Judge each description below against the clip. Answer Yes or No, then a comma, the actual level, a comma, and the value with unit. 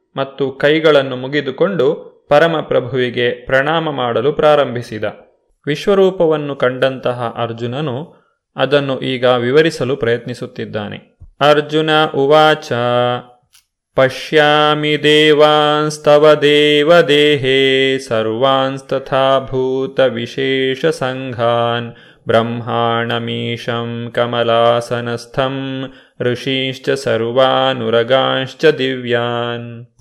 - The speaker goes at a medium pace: No, slow, 55 wpm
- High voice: No, low, 130 Hz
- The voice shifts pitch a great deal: No, average, 3.7 semitones